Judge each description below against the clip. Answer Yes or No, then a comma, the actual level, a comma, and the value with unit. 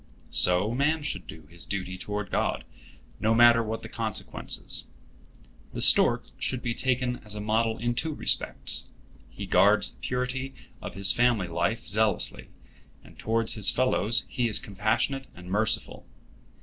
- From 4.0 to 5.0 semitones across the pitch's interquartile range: No, average, 3.3 semitones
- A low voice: Yes, low, 110 Hz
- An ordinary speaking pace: Yes, average, 150 wpm